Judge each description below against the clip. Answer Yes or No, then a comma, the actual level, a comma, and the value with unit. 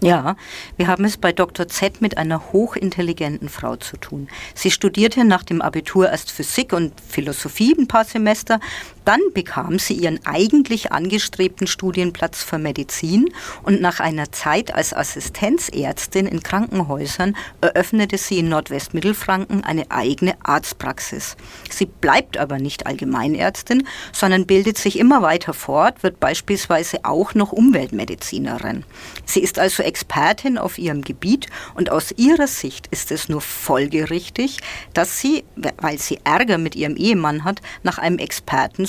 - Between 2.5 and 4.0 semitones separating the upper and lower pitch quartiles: No, average, 4.5 semitones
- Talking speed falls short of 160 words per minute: Yes, average, 140 wpm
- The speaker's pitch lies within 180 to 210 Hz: Yes, medium, 185 Hz